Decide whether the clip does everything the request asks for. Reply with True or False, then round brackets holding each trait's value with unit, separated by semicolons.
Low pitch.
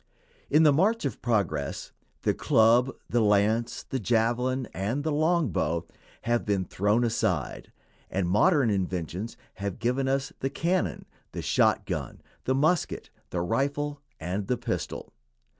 True (120 Hz)